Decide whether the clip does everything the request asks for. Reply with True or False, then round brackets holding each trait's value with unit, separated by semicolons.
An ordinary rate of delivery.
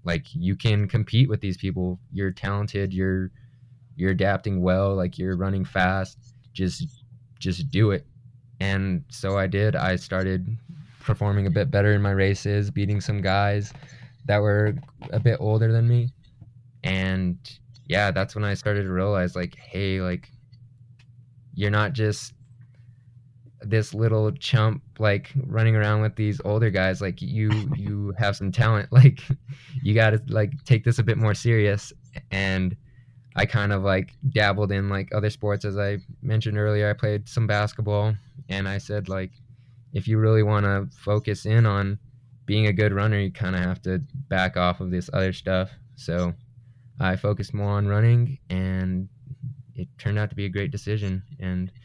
True (170 wpm)